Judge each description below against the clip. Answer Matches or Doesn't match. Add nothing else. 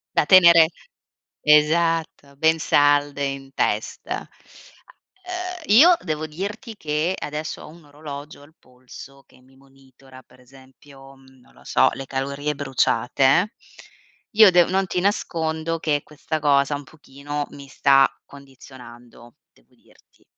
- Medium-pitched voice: Matches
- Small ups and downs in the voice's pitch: Doesn't match